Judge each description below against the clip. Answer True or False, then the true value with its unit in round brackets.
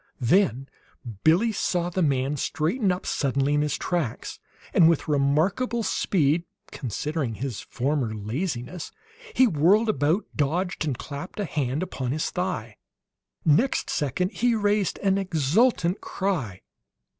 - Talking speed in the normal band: False (130 wpm)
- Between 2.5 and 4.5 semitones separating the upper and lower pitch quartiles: False (5.5 semitones)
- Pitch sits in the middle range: True (160 Hz)